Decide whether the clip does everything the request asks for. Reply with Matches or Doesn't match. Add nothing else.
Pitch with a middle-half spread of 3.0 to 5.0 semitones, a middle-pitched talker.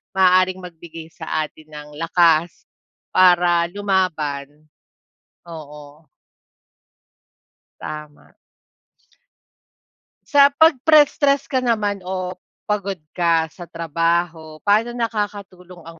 Matches